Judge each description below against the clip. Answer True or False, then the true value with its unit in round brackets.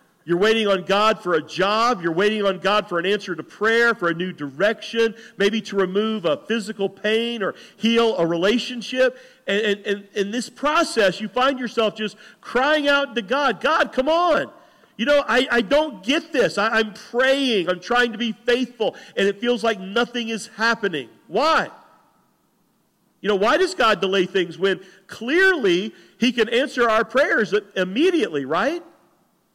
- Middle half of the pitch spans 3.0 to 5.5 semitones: True (3.9 semitones)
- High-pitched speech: True (225 Hz)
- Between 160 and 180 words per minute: True (175 wpm)